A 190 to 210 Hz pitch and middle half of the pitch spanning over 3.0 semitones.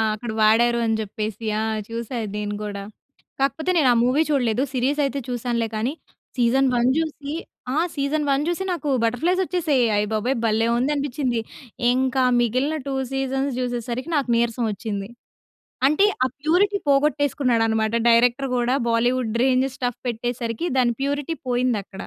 No: very high, 250 Hz; average, 3.4 semitones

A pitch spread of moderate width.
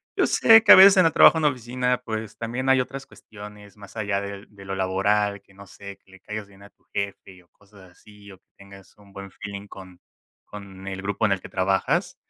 No: narrow, 2.1 semitones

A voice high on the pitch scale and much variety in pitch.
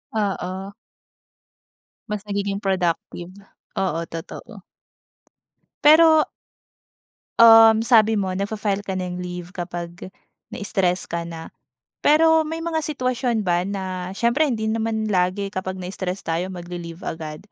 No: high, 195 Hz; average, 3.9 semitones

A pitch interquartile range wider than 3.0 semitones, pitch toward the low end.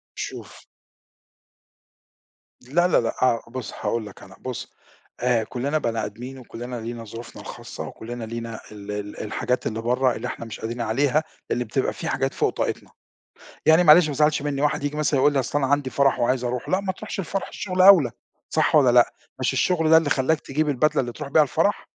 Yes: average, 4.5 semitones; low, 130 Hz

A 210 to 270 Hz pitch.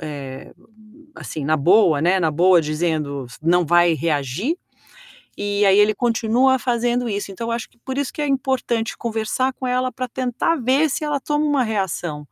Yes: high, 220 Hz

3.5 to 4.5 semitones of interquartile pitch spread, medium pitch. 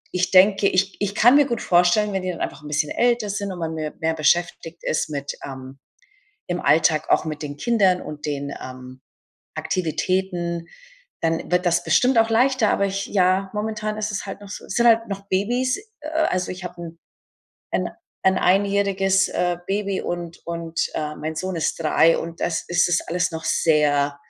Yes: average, 3.9 semitones; medium, 180 Hz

